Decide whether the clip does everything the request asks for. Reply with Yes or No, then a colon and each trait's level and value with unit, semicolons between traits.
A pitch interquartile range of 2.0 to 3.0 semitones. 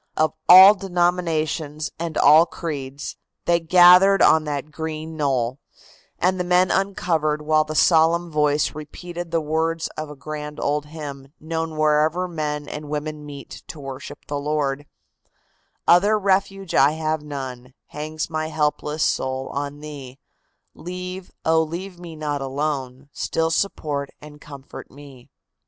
Yes: narrow, 2.4 semitones